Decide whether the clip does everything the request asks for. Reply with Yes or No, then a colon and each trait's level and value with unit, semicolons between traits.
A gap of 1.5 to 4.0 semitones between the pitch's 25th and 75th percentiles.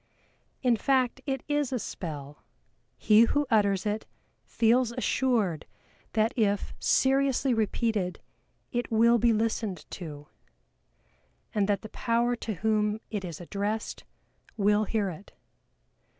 Yes: average, 3.0 semitones